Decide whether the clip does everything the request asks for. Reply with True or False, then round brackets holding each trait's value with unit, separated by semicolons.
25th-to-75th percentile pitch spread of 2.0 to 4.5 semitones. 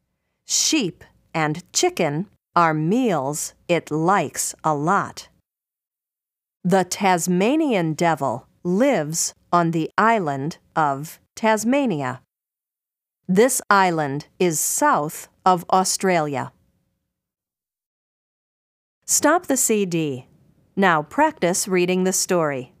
True (4.2 semitones)